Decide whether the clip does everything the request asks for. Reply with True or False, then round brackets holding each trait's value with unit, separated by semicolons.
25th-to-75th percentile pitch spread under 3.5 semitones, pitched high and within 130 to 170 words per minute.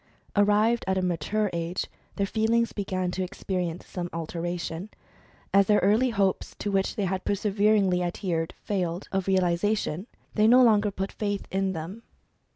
True (2.8 semitones; 195 Hz; 160 wpm)